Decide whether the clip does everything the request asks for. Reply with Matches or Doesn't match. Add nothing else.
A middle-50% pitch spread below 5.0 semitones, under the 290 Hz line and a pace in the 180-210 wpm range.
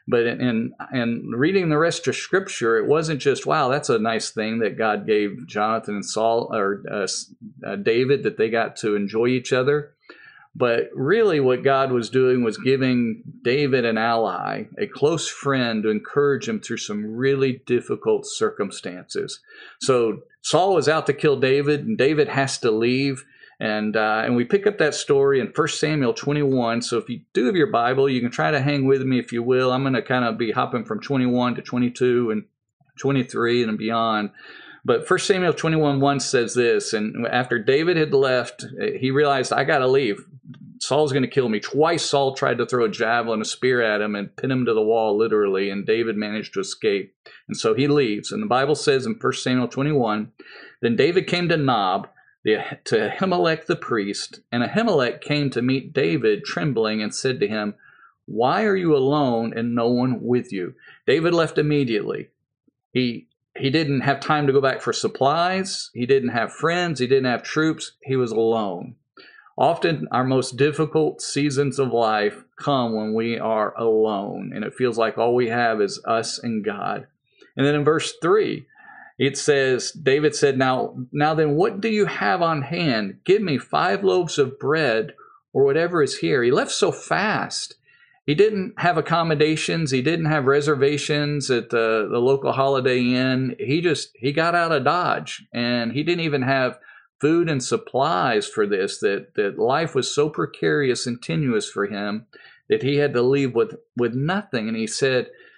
Doesn't match